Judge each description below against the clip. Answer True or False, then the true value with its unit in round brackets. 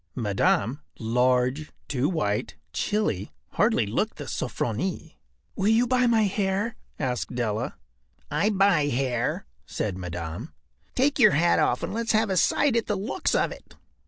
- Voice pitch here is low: False (155 Hz)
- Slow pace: False (150 wpm)